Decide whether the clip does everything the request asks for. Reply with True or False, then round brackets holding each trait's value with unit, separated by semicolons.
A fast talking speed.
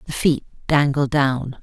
False (150 wpm)